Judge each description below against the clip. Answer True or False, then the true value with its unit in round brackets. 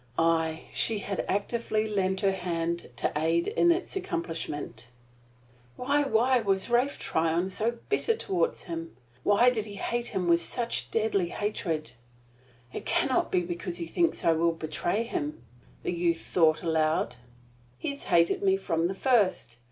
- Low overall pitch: False (185 Hz)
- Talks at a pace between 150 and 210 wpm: True (160 wpm)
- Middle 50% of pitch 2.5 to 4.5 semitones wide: False (5.6 semitones)